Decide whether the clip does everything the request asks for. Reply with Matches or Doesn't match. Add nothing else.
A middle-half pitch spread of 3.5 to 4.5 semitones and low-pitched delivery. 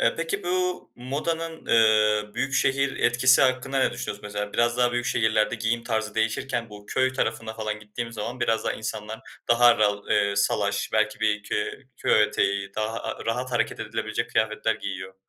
Doesn't match